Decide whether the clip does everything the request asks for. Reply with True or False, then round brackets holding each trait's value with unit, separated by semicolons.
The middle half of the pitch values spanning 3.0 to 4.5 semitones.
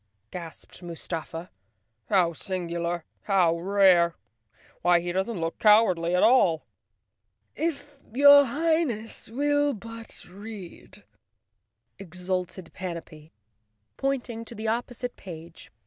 False (5.4 semitones)